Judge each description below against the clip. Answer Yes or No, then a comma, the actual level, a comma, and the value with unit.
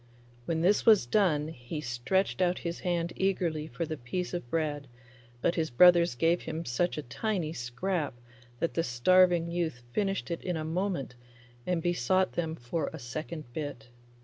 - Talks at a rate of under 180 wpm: Yes, average, 170 wpm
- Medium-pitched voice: Yes, medium, 165 Hz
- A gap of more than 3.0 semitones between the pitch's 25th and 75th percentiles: Yes, average, 3.5 semitones